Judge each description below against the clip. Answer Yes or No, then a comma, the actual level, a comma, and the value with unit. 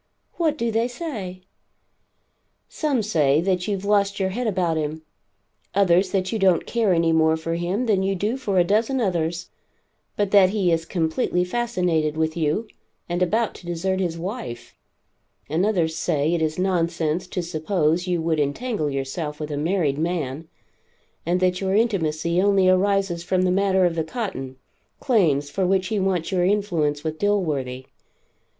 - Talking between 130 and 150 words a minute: No, average, 170 wpm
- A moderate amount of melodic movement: Yes, average, 3.8 semitones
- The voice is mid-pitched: Yes, medium, 180 Hz